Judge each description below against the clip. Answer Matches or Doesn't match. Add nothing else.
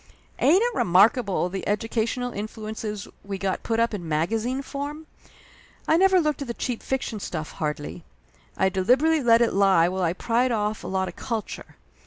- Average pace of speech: Matches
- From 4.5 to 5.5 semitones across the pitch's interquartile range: Matches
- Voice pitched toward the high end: Matches